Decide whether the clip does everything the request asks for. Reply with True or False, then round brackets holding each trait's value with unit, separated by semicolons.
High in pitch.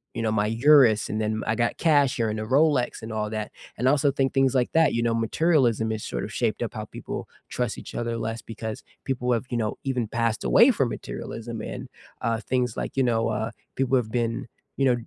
False (115 Hz)